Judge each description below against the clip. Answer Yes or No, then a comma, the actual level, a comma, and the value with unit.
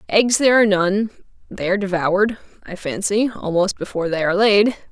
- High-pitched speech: Yes, high, 195 Hz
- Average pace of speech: Yes, average, 170 wpm